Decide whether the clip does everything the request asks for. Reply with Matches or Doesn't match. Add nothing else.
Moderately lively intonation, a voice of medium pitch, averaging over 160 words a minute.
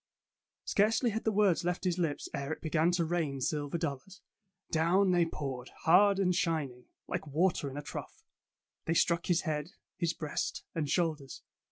Matches